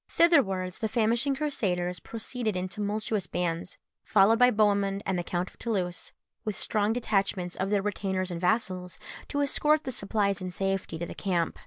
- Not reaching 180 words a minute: Yes, average, 170 wpm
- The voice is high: Yes, high, 200 Hz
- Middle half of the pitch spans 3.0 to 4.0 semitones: Yes, average, 3.4 semitones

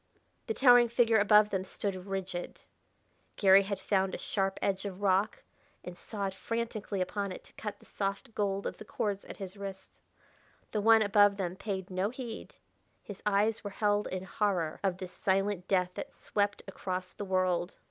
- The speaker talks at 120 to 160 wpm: No, average, 180 wpm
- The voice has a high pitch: Yes, high, 200 Hz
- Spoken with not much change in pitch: Yes, narrow, 1.8 semitones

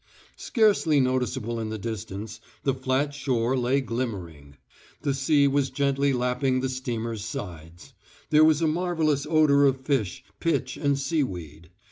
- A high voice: No, low, 130 Hz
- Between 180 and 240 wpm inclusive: No, average, 140 wpm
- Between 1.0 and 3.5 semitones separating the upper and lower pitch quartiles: No, average, 4.2 semitones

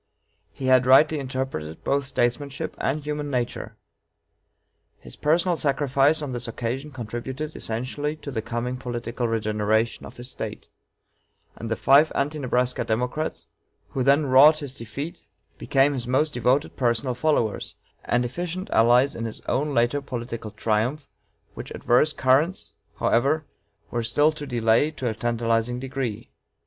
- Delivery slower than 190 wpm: Yes, average, 140 wpm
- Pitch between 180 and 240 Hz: No, low, 130 Hz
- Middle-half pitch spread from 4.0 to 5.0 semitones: No, average, 3.6 semitones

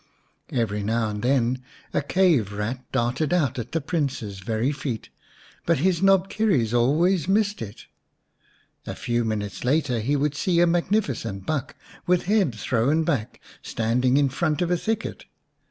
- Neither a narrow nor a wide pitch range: No, wide, 6.8 semitones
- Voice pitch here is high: No, low, 135 Hz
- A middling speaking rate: Yes, average, 155 wpm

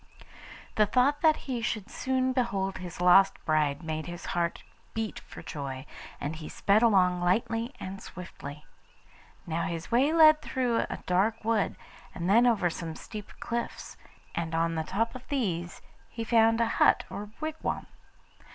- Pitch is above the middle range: Yes, high, 200 Hz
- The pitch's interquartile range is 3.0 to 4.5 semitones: No, wide, 5.6 semitones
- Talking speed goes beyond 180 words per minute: No, average, 160 wpm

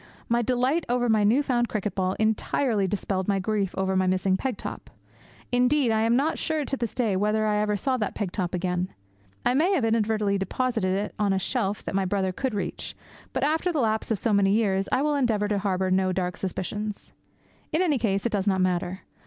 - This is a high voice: Yes, high, 210 Hz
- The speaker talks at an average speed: No, fast, 220 wpm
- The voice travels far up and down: No, average, 4.1 semitones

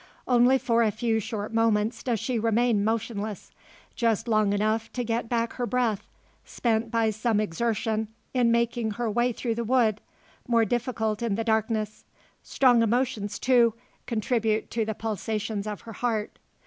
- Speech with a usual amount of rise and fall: No, narrow, 1.7 semitones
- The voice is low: No, high, 225 Hz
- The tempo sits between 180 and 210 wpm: No, average, 160 wpm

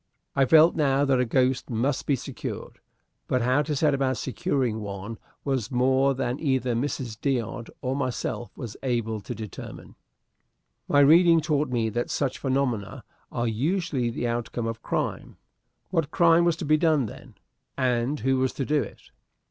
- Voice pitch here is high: No, low, 130 Hz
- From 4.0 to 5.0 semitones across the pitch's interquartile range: No, average, 3.4 semitones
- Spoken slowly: No, average, 165 wpm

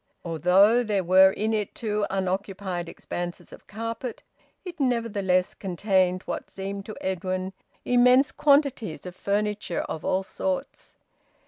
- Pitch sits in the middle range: No, high, 200 Hz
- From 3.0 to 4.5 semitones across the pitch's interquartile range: Yes, average, 3.6 semitones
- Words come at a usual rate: No, slow, 125 wpm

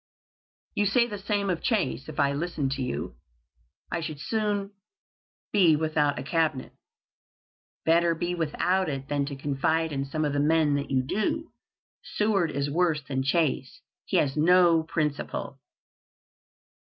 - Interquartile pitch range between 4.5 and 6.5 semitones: No, average, 3.9 semitones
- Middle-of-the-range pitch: Yes, medium, 155 Hz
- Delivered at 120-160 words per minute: Yes, average, 150 wpm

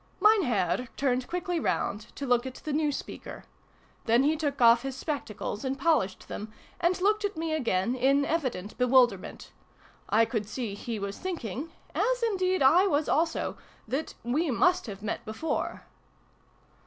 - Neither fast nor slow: Yes, average, 165 wpm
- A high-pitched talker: Yes, very high, 270 Hz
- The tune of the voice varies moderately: No, wide, 6.2 semitones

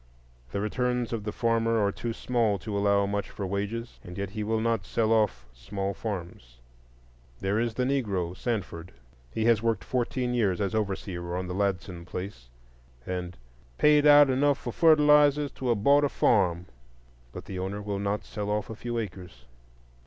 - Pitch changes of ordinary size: Yes, average, 3.7 semitones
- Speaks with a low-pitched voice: Yes, low, 105 Hz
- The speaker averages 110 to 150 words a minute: No, average, 175 wpm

